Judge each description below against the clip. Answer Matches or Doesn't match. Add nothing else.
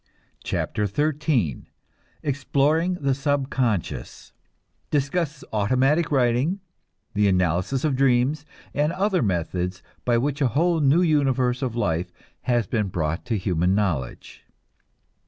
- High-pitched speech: Doesn't match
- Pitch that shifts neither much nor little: Doesn't match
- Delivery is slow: Matches